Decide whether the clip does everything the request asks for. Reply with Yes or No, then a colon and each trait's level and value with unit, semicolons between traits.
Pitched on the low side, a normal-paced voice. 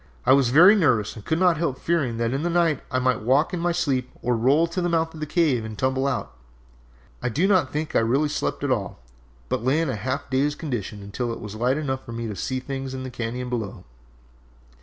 No: low, 130 Hz; fast, 245 wpm